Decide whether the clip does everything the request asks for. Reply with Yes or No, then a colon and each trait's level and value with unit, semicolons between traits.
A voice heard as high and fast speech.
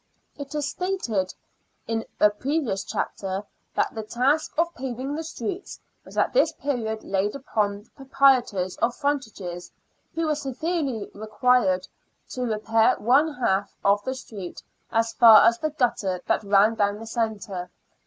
No: high, 230 Hz; average, 155 wpm